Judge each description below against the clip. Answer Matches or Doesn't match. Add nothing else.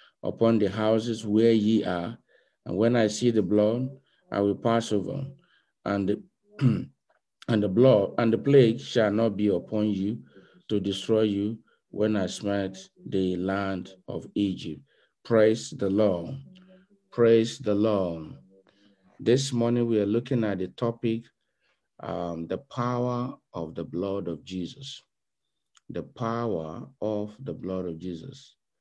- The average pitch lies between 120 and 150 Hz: Doesn't match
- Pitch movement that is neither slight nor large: Matches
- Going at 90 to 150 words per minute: Matches